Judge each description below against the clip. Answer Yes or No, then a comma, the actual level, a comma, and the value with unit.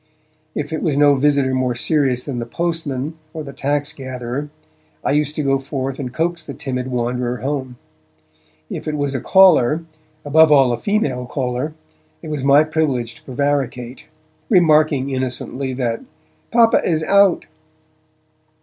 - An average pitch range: Yes, average, 3.2 semitones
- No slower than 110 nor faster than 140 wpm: No, average, 150 wpm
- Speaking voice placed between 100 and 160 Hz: Yes, medium, 140 Hz